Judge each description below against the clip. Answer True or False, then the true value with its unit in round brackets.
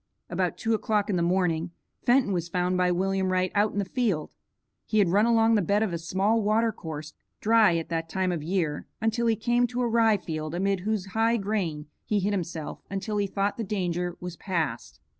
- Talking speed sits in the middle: False (215 wpm)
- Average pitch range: True (3.9 semitones)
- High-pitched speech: True (195 Hz)